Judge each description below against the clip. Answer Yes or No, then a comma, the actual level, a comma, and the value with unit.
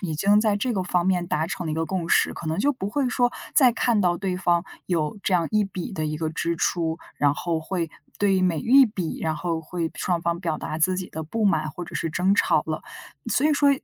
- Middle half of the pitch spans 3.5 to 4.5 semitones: Yes, average, 3.8 semitones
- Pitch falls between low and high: Yes, medium, 180 Hz